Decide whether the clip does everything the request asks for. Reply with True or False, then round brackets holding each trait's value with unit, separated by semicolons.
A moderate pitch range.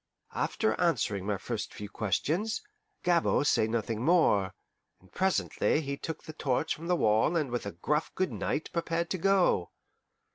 False (8.1 semitones)